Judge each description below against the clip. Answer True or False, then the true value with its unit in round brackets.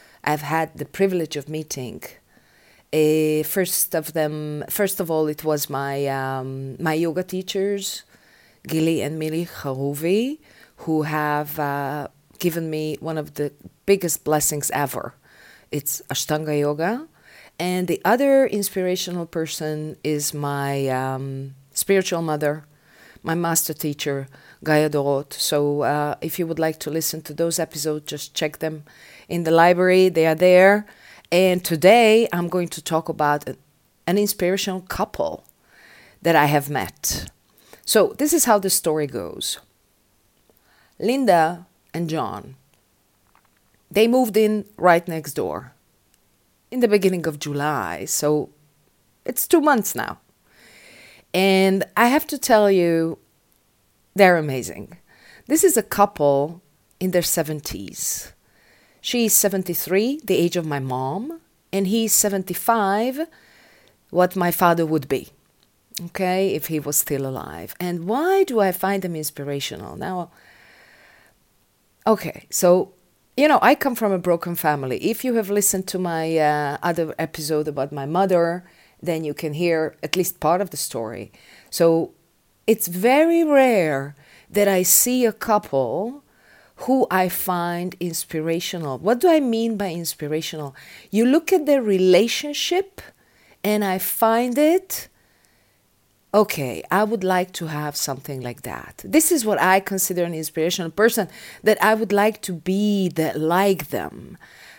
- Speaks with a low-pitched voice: False (170 Hz)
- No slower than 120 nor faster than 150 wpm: True (140 wpm)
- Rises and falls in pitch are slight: False (4.7 semitones)